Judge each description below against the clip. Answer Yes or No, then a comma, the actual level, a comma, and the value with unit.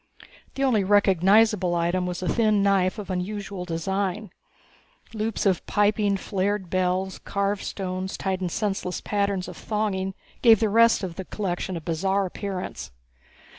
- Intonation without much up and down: Yes, narrow, 2.1 semitones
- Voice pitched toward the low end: No, high, 195 Hz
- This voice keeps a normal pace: Yes, average, 145 wpm